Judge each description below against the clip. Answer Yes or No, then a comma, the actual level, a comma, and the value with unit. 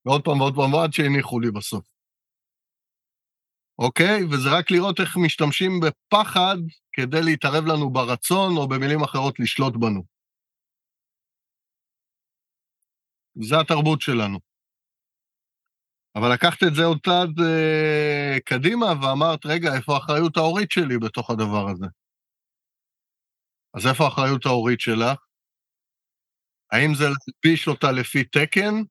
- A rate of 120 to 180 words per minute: No, average, 110 wpm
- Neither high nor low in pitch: Yes, medium, 150 Hz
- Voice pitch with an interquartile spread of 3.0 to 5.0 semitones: Yes, average, 4.4 semitones